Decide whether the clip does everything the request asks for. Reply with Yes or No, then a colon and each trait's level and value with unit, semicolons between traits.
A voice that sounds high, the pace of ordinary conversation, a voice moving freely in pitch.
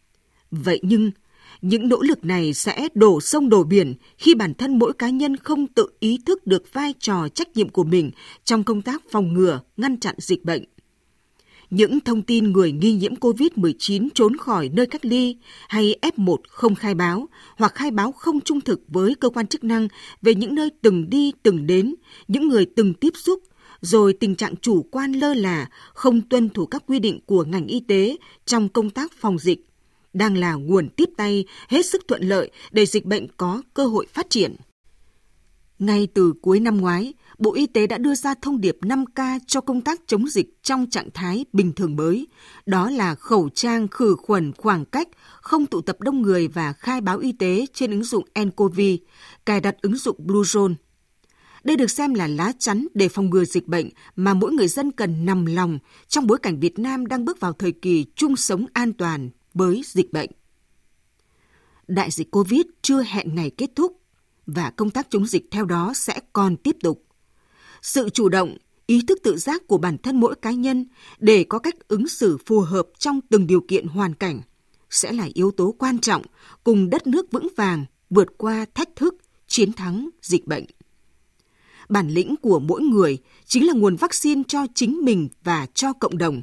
Yes: high, 210 Hz; average, 195 wpm; wide, 6.0 semitones